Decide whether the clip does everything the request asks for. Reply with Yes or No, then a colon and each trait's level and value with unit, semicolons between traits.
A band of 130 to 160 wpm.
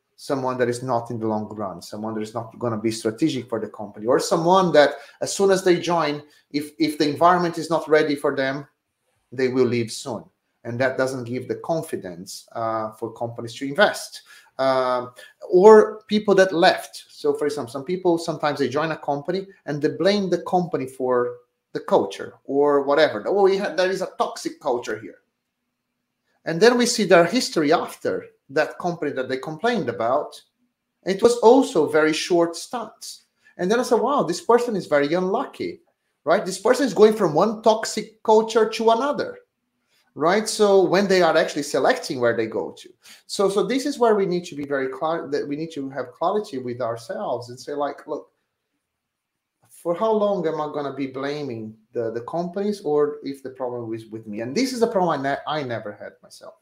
No: average, 200 wpm